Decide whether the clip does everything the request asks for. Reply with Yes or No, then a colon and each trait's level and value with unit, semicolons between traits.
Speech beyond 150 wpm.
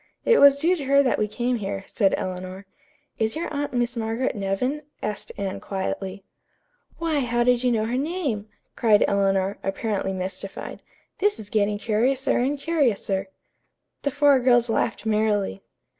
Yes: average, 160 wpm